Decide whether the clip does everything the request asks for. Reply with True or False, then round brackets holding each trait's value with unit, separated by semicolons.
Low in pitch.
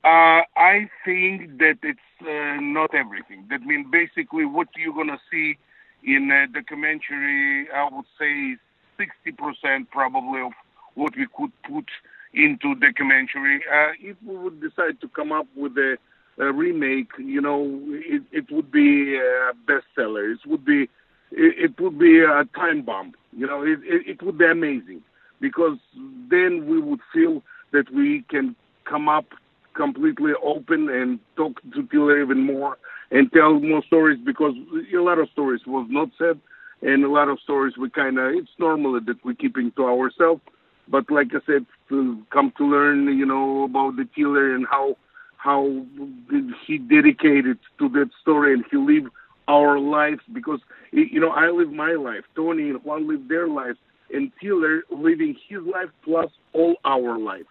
False (160 Hz)